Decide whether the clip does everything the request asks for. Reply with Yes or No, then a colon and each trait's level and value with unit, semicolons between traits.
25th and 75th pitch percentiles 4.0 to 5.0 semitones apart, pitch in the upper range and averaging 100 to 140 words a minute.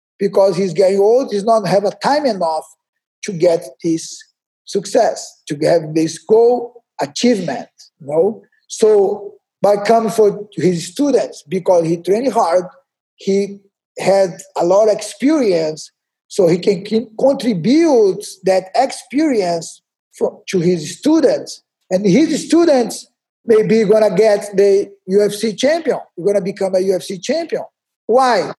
Yes: average, 4.7 semitones; high, 205 Hz; slow, 135 wpm